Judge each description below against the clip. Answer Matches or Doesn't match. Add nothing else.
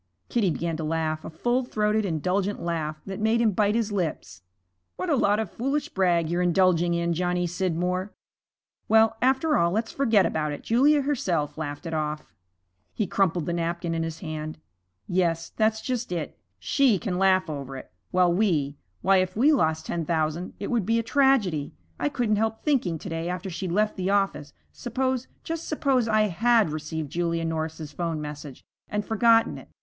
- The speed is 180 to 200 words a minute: Matches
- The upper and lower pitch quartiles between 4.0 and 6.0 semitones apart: Matches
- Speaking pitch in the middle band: Matches